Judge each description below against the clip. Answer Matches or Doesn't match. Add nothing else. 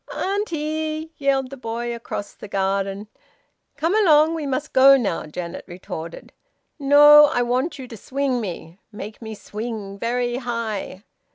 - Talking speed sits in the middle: Matches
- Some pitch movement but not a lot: Doesn't match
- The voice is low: Doesn't match